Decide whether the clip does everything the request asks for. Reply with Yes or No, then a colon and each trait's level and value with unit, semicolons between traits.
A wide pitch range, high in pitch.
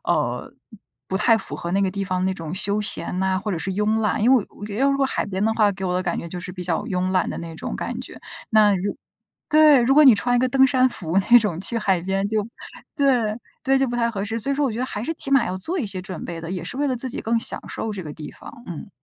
No: average, 4.7 semitones; high, 210 Hz